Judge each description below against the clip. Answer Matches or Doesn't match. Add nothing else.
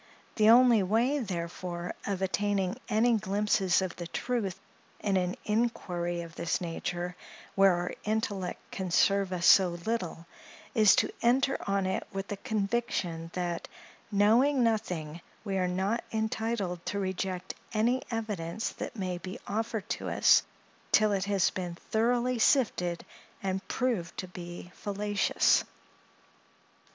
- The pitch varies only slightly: Doesn't match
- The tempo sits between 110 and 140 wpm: Matches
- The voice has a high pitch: Matches